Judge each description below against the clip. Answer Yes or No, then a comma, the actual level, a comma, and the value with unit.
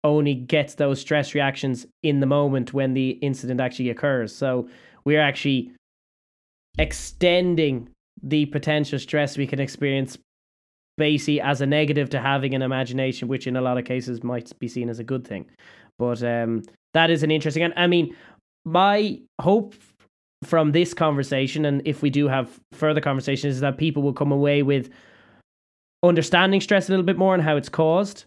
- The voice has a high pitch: No, medium, 140 Hz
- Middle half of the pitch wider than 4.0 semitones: No, average, 3.1 semitones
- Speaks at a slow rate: No, average, 175 wpm